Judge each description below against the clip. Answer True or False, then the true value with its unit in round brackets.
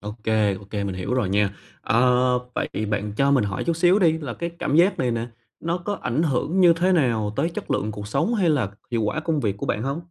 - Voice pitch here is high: False (125 Hz)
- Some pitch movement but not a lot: False (7.7 semitones)